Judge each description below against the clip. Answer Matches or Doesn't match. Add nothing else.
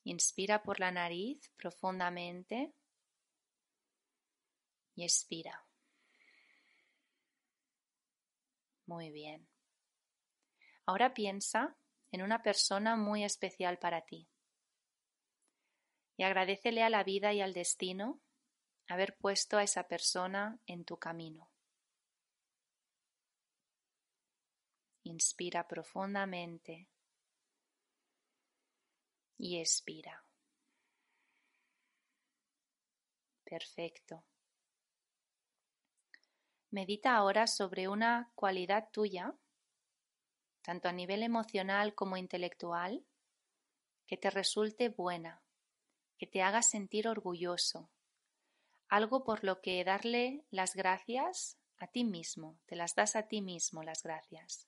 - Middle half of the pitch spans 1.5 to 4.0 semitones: Doesn't match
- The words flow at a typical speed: Doesn't match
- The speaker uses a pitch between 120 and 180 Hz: Doesn't match